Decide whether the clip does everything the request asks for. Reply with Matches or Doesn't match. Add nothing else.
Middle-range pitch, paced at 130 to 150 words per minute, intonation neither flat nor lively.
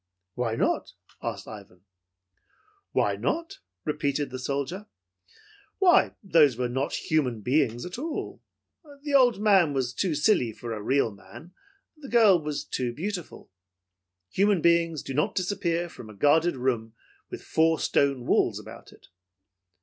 Doesn't match